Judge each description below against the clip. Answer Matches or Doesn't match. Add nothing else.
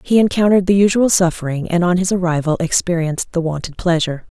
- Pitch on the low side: Doesn't match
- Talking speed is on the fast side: Doesn't match